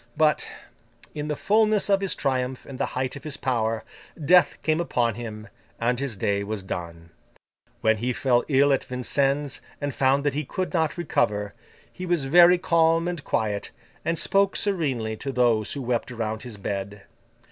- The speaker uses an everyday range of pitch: No, wide, 6.2 semitones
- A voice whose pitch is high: No, low, 135 Hz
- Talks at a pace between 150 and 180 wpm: Yes, average, 175 wpm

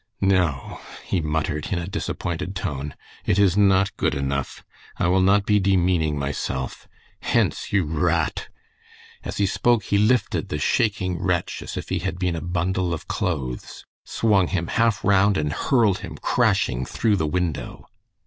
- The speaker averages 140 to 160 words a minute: No, average, 175 wpm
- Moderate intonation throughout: Yes, average, 4.1 semitones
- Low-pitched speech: Yes, very low, 90 Hz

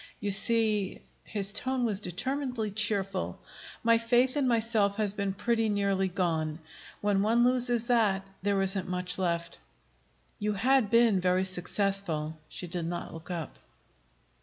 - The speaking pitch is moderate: No, high, 200 Hz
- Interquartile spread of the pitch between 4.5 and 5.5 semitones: No, average, 3.8 semitones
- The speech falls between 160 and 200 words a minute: No, average, 140 wpm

